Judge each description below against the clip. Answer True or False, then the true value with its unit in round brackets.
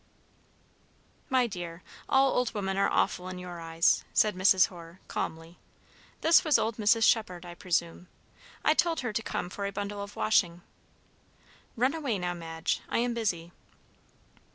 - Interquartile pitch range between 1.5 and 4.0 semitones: False (4.7 semitones)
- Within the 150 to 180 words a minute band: True (155 wpm)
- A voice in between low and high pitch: False (195 Hz)